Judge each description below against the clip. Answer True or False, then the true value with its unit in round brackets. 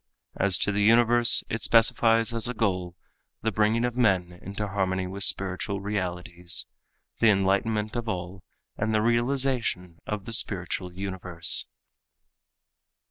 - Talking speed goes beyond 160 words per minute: False (135 wpm)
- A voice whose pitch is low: True (100 Hz)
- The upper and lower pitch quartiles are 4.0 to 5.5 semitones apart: False (3.6 semitones)